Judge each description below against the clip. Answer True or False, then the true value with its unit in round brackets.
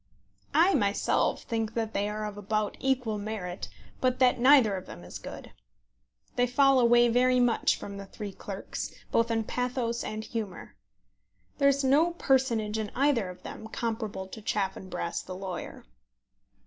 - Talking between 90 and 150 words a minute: False (160 wpm)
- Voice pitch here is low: False (225 Hz)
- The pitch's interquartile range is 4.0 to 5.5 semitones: False (3.6 semitones)